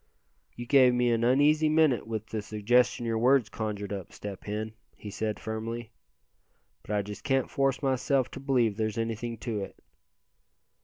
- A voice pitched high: No, low, 115 Hz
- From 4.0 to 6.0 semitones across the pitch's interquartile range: No, average, 3.2 semitones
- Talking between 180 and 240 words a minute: No, average, 165 wpm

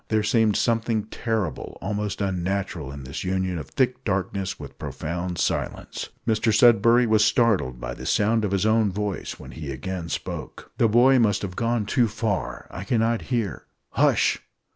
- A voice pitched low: Yes, low, 105 Hz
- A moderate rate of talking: Yes, average, 170 wpm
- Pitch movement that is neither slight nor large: Yes, average, 3.6 semitones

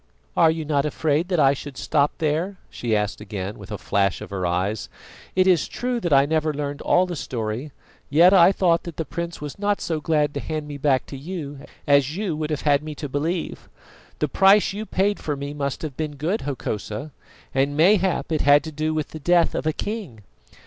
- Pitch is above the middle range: No, medium, 150 Hz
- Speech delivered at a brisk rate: Yes, fast, 220 wpm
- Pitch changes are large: No, average, 3.4 semitones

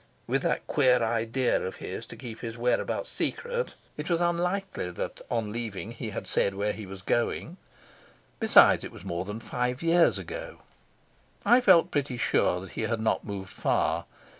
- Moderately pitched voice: No, low, 120 Hz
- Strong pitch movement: Yes, wide, 8.1 semitones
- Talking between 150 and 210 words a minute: Yes, average, 175 wpm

